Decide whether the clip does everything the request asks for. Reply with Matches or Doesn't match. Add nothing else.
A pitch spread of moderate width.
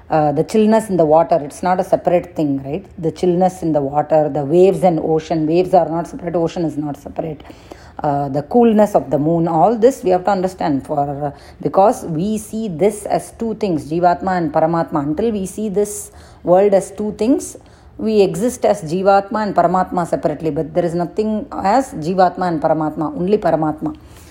Matches